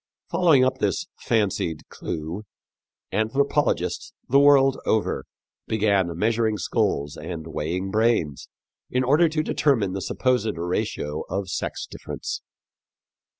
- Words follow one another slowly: Yes, slow, 110 wpm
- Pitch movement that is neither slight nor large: No, wide, 6.7 semitones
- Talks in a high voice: No, low, 110 Hz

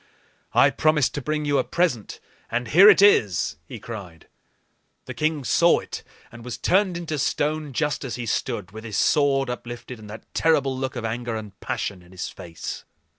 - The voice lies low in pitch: Yes, low, 125 Hz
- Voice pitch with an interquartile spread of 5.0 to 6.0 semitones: Yes, wide, 5.5 semitones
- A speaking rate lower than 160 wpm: No, average, 185 wpm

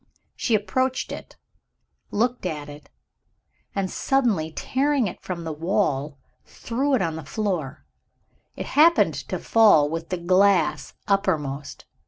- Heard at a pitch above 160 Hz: Yes, high, 190 Hz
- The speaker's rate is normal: No, slow, 130 wpm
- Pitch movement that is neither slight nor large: No, wide, 6.8 semitones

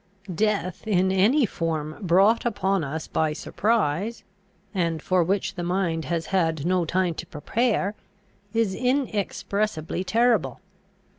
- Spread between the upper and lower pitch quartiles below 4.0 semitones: No, average, 4.4 semitones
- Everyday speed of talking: No, slow, 125 wpm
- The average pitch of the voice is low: No, medium, 185 Hz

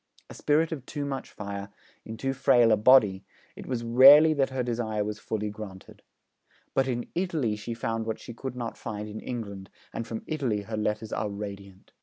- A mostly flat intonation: No, average, 3.9 semitones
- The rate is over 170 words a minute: Yes, average, 195 wpm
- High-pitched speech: No, low, 115 Hz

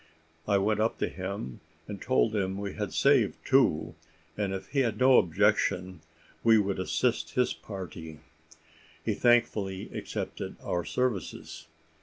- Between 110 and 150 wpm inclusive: Yes, slow, 135 wpm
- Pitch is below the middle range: Yes, low, 100 Hz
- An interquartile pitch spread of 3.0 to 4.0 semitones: Yes, average, 3.3 semitones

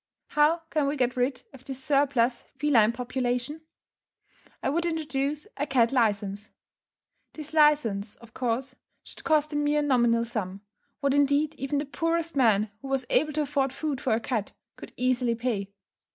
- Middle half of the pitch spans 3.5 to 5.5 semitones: Yes, average, 3.9 semitones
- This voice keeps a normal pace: Yes, average, 165 wpm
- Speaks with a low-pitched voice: No, very high, 270 Hz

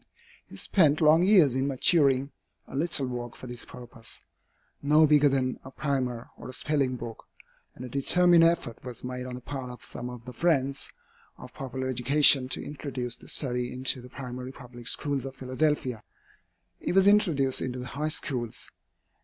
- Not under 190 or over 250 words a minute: No, average, 175 wpm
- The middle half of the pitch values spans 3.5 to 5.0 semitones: No, average, 2.8 semitones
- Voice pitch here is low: Yes, low, 130 Hz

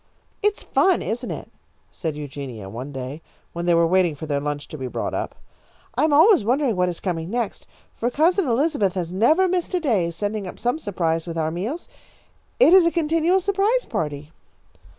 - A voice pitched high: Yes, high, 200 Hz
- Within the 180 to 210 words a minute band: Yes, average, 190 wpm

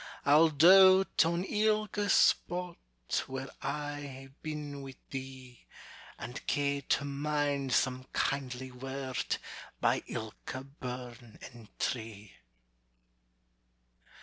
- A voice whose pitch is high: No, medium, 140 Hz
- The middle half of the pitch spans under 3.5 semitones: Yes, average, 2.8 semitones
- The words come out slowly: Yes, slow, 95 wpm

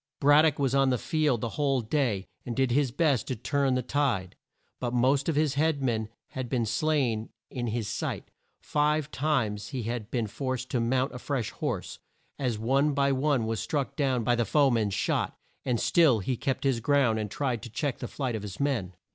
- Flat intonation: No, average, 3.5 semitones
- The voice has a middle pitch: No, low, 130 Hz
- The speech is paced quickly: Yes, fast, 210 wpm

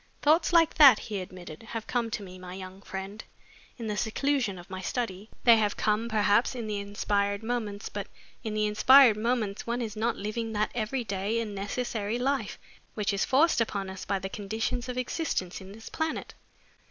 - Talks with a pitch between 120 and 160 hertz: No, high, 215 Hz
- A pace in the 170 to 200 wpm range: Yes, average, 190 wpm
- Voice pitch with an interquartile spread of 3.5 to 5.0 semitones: No, average, 3.0 semitones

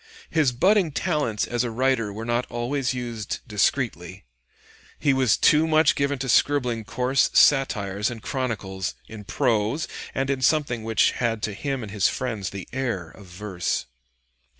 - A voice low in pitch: Yes, low, 120 Hz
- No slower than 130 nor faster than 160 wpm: Yes, average, 155 wpm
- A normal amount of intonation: Yes, average, 4.3 semitones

